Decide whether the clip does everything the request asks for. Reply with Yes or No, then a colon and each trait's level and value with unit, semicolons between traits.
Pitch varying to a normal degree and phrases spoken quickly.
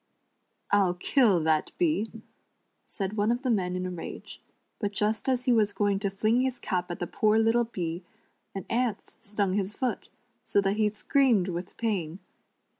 No: average, 3.8 semitones; average, 180 wpm